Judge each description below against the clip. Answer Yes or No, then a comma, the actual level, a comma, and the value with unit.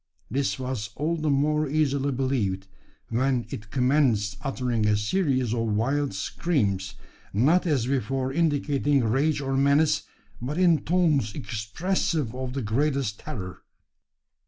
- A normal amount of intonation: Yes, average, 4.7 semitones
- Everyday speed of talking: No, slow, 130 wpm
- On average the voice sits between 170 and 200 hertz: No, low, 135 Hz